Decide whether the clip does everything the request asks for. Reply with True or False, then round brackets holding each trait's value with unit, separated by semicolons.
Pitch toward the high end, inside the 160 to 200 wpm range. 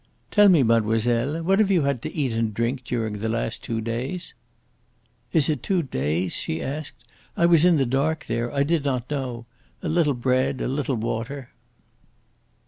False (130 Hz; 180 wpm)